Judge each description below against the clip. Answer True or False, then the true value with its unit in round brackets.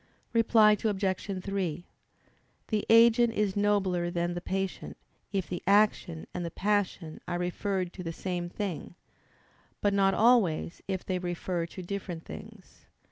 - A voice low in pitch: False (190 Hz)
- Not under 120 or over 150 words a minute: True (140 wpm)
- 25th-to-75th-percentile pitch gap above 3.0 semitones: False (2.7 semitones)